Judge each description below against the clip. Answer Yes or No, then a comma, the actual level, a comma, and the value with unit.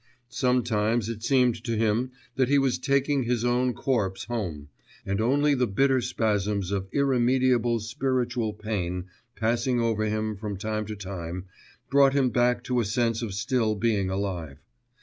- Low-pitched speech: Yes, low, 115 Hz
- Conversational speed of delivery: Yes, average, 155 wpm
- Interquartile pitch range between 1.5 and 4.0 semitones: Yes, average, 3.3 semitones